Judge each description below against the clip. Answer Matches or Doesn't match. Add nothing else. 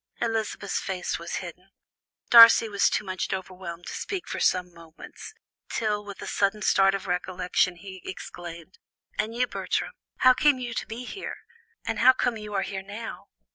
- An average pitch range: Matches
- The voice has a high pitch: Matches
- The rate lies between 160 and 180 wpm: Matches